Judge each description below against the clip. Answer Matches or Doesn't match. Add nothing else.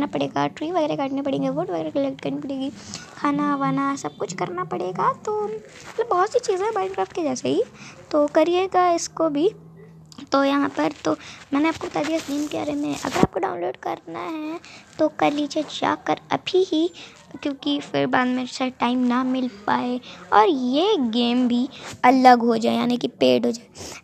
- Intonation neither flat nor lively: Matches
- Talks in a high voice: Matches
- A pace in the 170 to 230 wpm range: Matches